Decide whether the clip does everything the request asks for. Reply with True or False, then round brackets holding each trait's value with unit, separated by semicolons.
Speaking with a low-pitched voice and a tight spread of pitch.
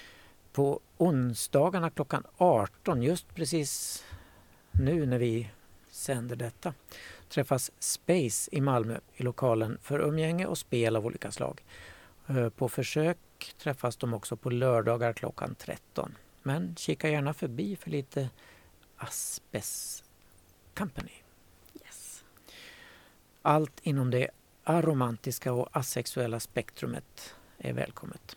False (125 Hz; 4.8 semitones)